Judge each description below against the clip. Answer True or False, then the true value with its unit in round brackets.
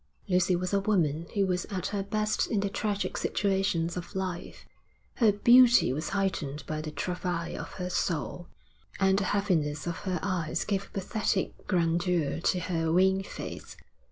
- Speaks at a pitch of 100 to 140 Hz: False (185 Hz)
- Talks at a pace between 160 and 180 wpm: True (165 wpm)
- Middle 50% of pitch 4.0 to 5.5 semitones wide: False (2.9 semitones)